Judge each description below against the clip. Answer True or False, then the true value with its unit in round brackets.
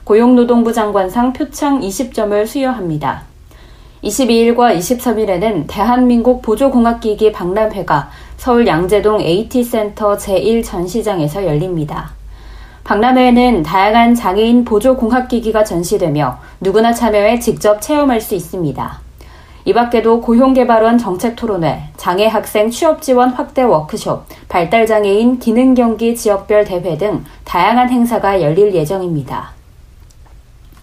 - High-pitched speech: True (215 Hz)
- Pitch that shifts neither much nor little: True (4.5 semitones)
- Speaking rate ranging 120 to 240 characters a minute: False (290 characters per minute)